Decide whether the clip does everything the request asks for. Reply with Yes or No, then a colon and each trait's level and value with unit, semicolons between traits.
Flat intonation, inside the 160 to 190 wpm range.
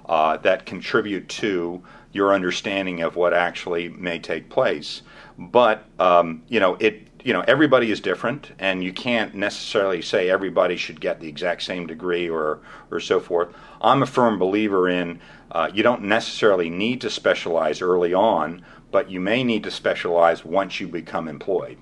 Yes: narrow, 1.2 semitones; average, 170 wpm